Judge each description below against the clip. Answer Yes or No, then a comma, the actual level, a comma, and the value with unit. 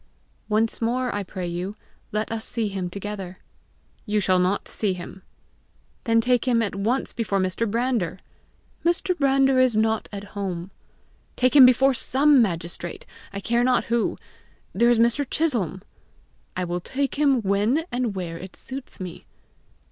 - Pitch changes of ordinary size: Yes, average, 4.8 semitones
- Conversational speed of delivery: Yes, average, 155 wpm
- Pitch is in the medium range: No, high, 220 Hz